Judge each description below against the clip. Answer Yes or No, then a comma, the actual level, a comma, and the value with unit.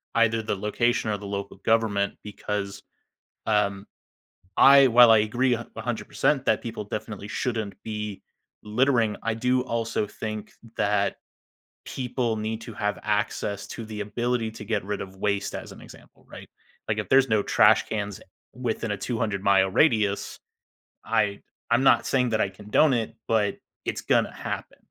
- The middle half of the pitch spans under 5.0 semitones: Yes, narrow, 2.4 semitones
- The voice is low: Yes, low, 110 Hz